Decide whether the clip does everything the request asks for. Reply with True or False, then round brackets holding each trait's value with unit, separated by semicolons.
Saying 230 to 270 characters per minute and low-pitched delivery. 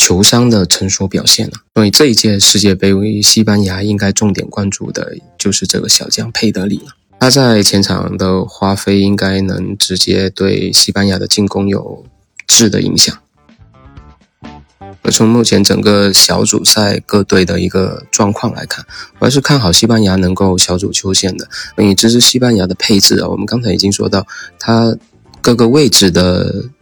True (265 characters per minute; 100 Hz)